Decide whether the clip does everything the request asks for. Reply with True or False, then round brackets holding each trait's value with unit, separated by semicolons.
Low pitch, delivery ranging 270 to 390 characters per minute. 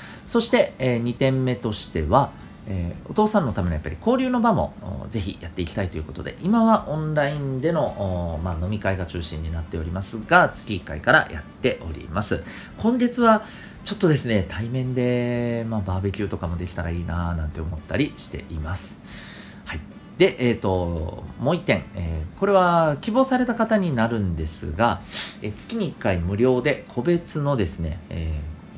True (110 Hz; 355 characters per minute)